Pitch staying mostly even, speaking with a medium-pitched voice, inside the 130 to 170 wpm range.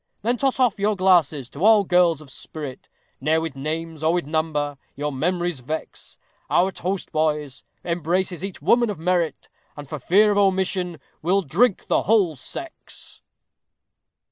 No: average, 4.0 semitones; medium, 170 Hz; average, 155 wpm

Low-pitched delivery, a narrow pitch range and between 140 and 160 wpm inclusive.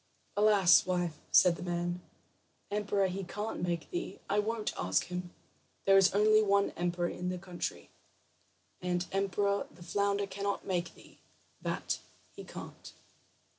No: high, 190 Hz; narrow, 2.3 semitones; average, 145 wpm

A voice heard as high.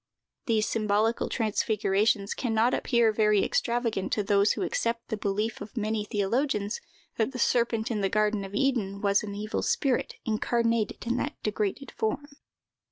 Yes: high, 220 Hz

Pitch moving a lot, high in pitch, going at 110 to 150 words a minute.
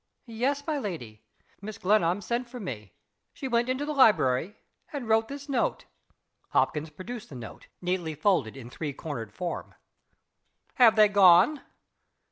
Yes: wide, 7.8 semitones; high, 205 Hz; average, 145 wpm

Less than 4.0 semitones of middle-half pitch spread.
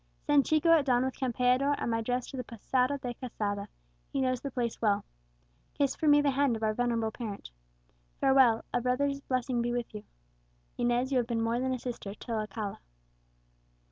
Yes: average, 2.8 semitones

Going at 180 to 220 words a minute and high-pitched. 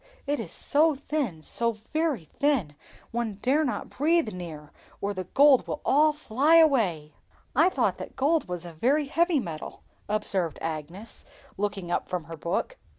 No: average, 160 wpm; high, 235 Hz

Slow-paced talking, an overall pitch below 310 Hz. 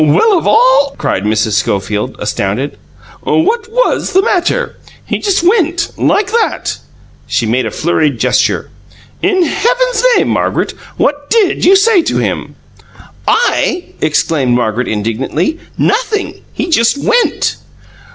No: slow, 130 wpm; very high, 325 Hz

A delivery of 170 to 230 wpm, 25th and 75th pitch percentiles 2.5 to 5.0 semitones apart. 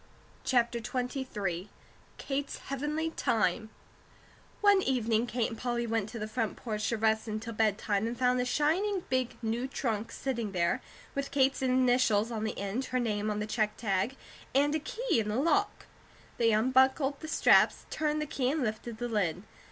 Yes: average, 175 wpm; average, 3.7 semitones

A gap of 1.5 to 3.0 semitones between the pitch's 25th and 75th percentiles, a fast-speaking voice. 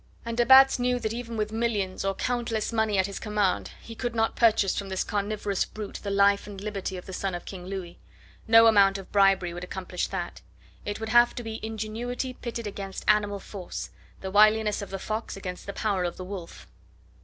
Yes: narrow, 2.5 semitones; fast, 210 wpm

